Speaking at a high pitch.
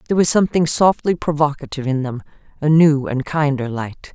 No: medium, 145 Hz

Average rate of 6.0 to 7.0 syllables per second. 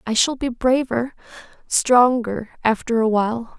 No: 4.3 syllables/s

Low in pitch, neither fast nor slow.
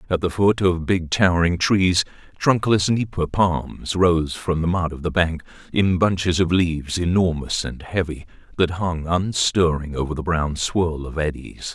Yes: very low, 85 Hz; average, 170 wpm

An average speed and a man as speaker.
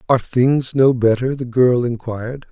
Yes: average, 165 wpm; male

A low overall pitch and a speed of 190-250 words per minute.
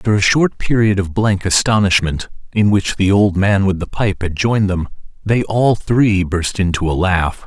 Yes: low, 100 Hz; average, 200 wpm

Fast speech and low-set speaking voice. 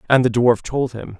Yes: fast, 250 wpm; low, 120 Hz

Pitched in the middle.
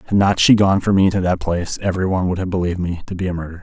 No: very low, 90 Hz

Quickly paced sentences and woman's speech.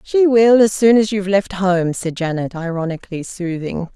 No: average, 180 wpm; female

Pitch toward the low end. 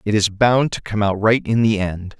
Yes: low, 105 Hz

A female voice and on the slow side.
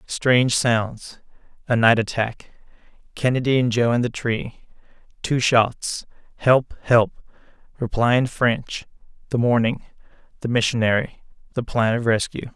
No: male; slow, 85 wpm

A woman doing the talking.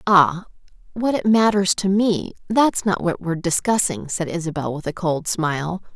Yes: female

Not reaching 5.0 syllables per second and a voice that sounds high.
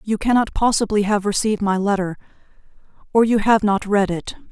No: 5.8 syllables/s; high, 205 Hz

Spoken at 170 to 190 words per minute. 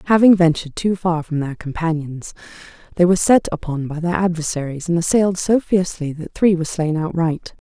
Yes: average, 180 wpm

